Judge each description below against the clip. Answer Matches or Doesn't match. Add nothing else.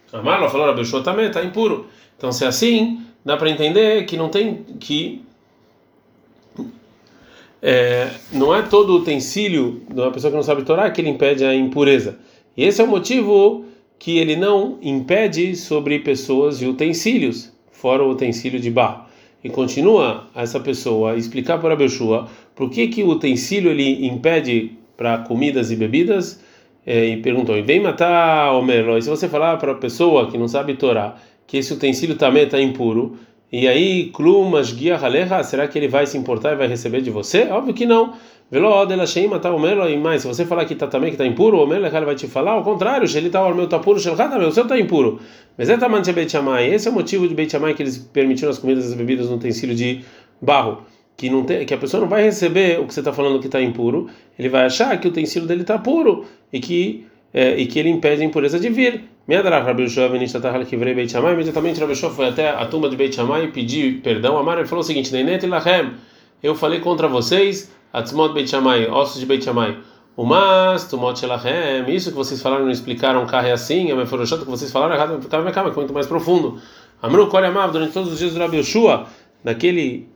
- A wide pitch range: Matches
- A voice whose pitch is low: Doesn't match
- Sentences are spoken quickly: Matches